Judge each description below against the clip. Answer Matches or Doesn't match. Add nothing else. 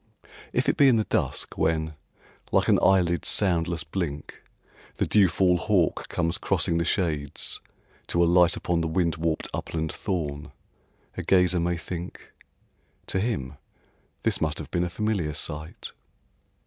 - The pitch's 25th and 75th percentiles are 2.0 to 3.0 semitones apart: Matches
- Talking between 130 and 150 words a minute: Matches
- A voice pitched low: Matches